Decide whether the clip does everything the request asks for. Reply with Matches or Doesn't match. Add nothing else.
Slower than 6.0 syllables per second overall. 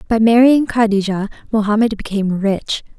Matches